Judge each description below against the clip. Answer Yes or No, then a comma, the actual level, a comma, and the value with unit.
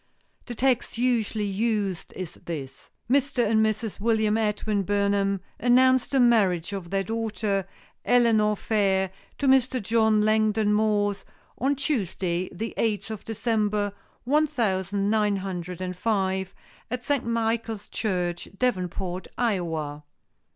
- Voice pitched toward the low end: No, high, 210 Hz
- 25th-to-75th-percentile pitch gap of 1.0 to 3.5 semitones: Yes, average, 3.2 semitones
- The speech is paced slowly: Yes, slow, 125 wpm